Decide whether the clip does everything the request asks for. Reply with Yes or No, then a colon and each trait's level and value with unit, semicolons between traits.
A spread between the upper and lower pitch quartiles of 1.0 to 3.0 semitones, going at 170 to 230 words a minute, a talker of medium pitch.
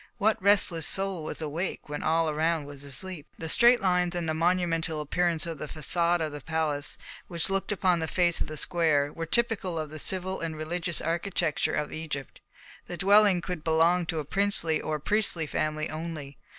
Yes: average, 2.7 semitones; average, 190 wpm; medium, 165 Hz